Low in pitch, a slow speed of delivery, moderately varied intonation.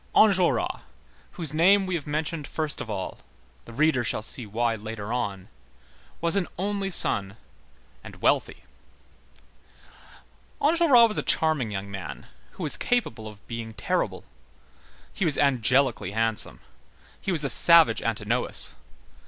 No: low, 130 Hz; slow, 130 wpm; wide, 7.8 semitones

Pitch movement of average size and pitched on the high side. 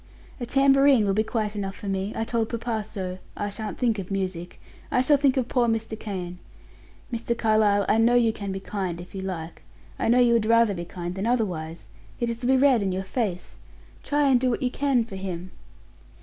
Yes: average, 3.9 semitones; high, 215 Hz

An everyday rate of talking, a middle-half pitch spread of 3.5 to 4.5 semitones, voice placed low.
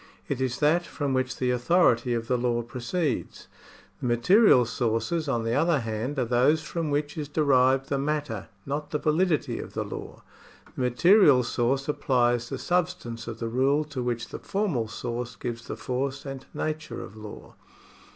Yes: average, 175 wpm; average, 4.0 semitones; low, 130 Hz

